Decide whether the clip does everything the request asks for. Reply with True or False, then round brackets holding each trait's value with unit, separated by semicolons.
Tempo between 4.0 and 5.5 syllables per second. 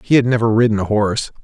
False (7.3 syllables/s)